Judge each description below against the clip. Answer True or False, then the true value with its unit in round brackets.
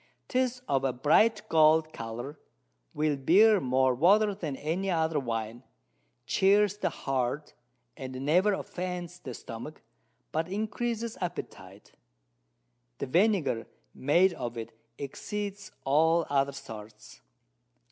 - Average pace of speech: False (115 wpm)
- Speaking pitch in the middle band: True (155 Hz)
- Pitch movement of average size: False (6.7 semitones)